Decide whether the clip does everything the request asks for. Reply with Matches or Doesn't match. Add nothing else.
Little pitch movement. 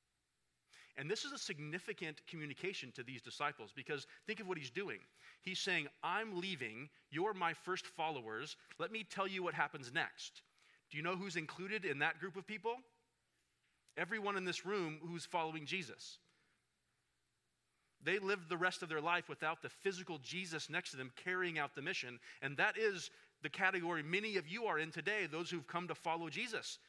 Doesn't match